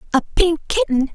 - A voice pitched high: Yes, very high, 325 Hz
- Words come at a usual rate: Yes, average, 155 wpm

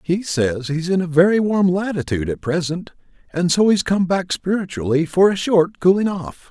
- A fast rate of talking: No, average, 195 wpm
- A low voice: No, medium, 175 Hz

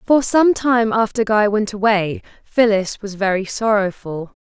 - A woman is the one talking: Yes, female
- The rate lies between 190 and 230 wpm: No, average, 150 wpm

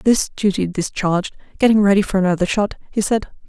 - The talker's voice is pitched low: No, high, 200 Hz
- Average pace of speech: Yes, average, 170 wpm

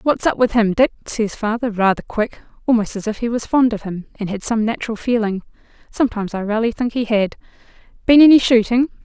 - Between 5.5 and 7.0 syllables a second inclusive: Yes, 6.0 syllables/s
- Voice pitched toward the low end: No, high, 225 Hz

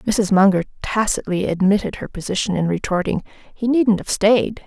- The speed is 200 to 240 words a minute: No, average, 155 wpm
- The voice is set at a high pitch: Yes, high, 200 Hz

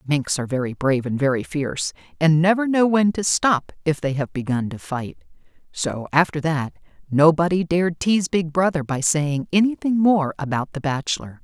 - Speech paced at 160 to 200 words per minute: Yes, average, 180 wpm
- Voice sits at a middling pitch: Yes, medium, 155 Hz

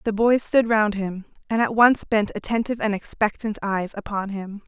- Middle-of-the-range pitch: No, high, 210 Hz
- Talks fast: No, average, 195 wpm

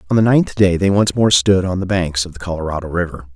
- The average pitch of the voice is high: No, very low, 90 Hz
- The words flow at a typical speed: No, fast, 270 wpm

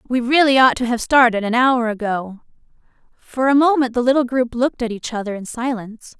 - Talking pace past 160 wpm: Yes, fast, 205 wpm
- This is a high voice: Yes, high, 245 Hz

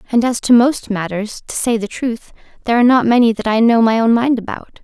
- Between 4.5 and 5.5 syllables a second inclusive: No, 5.9 syllables/s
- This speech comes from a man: No, female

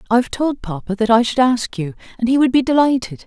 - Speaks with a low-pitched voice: No, high, 240 Hz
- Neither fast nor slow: No, fast, 255 wpm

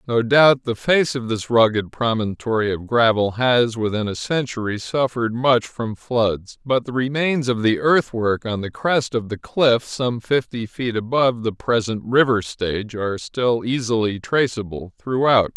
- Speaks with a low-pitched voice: Yes, low, 115 Hz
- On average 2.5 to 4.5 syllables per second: Yes, 4.4 syllables/s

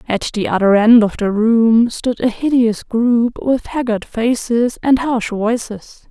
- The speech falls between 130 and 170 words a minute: Yes, average, 165 wpm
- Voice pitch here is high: Yes, high, 230 Hz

